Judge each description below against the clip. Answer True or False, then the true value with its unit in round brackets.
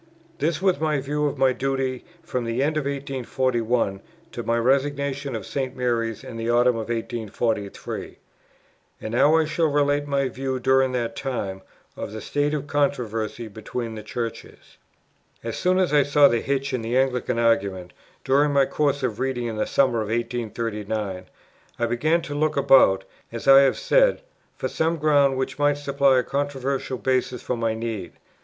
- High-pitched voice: False (130 Hz)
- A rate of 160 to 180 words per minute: True (175 wpm)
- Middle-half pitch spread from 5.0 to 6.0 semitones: False (3.6 semitones)